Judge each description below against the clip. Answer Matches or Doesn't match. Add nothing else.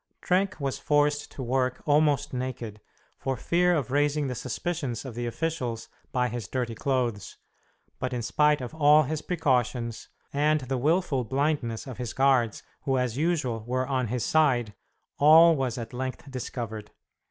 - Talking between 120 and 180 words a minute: Matches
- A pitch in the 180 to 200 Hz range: Doesn't match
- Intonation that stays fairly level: Doesn't match